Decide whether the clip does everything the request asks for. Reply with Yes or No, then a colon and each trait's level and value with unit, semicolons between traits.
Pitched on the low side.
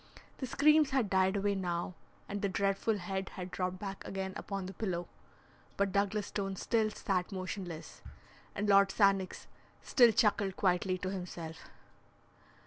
No: high, 195 Hz